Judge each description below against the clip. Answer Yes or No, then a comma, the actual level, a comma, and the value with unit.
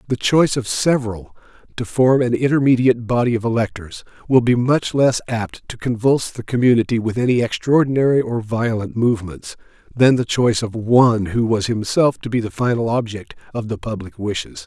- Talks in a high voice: No, low, 115 Hz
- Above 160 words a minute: Yes, average, 175 wpm